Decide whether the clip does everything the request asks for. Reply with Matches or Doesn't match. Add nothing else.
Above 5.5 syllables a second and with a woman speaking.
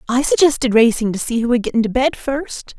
Matches